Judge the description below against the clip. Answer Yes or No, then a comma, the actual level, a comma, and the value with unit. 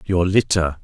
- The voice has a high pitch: No, very low, 90 Hz